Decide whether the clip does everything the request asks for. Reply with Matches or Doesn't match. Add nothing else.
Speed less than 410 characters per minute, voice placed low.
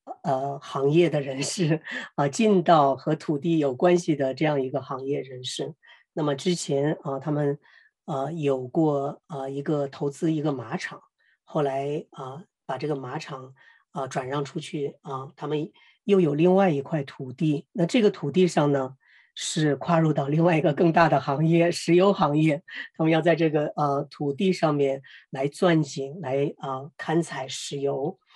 Doesn't match